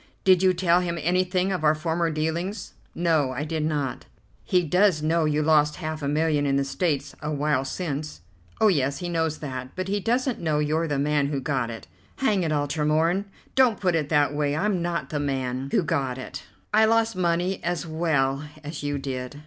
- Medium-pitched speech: Yes, medium, 155 Hz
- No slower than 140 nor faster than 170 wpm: No, fast, 205 wpm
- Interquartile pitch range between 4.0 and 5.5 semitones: No, average, 3.5 semitones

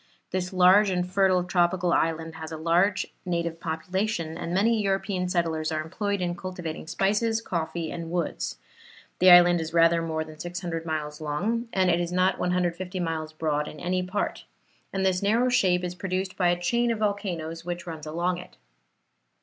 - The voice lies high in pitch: No, medium, 175 Hz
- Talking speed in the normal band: Yes, average, 175 wpm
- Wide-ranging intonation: No, narrow, 2.5 semitones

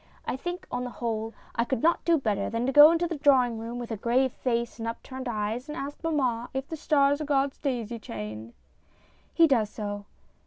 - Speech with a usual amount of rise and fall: Yes, average, 3.9 semitones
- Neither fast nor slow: No, fast, 210 wpm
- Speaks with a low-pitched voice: No, high, 245 Hz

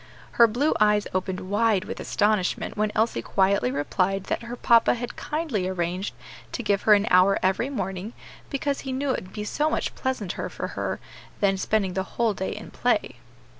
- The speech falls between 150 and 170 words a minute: No, average, 185 wpm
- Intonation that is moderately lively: Yes, average, 3.8 semitones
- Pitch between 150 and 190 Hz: No, high, 210 Hz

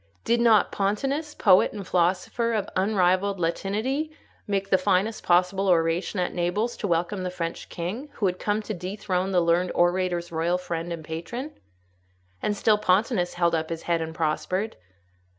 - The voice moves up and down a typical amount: Yes, average, 3.3 semitones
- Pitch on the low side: No, medium, 185 Hz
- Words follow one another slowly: No, average, 165 wpm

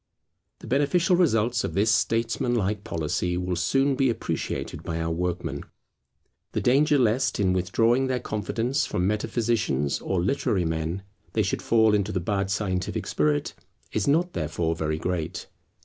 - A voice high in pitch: No, low, 105 Hz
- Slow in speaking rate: No, average, 150 wpm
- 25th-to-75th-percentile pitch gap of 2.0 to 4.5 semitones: No, wide, 5.4 semitones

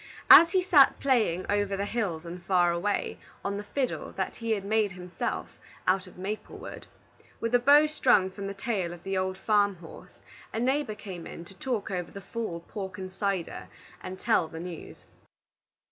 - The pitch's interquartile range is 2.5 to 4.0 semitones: Yes, average, 3.6 semitones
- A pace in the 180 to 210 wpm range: Yes, average, 190 wpm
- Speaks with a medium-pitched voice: No, high, 200 Hz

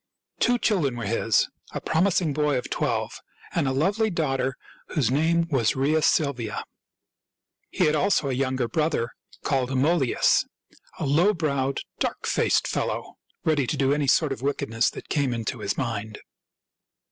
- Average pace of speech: Yes, average, 160 wpm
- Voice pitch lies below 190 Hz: Yes, medium, 140 Hz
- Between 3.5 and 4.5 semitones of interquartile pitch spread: Yes, average, 3.8 semitones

